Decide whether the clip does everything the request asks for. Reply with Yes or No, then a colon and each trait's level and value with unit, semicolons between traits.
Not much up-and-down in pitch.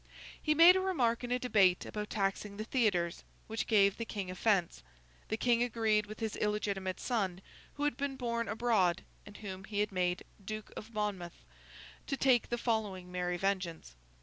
No: average, 3.7 semitones